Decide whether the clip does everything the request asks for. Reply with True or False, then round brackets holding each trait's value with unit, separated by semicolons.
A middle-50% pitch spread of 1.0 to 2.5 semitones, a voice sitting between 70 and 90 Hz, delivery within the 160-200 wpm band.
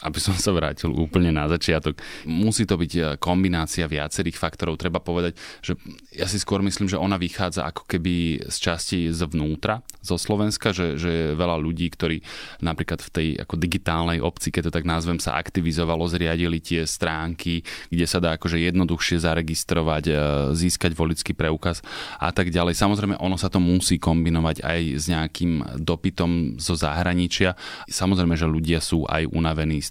True (1.8 semitones; 85 Hz; 165 wpm)